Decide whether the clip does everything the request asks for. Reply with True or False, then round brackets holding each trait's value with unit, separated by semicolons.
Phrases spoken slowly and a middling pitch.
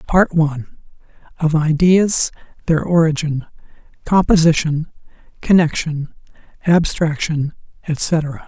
True (70 wpm; 160 Hz)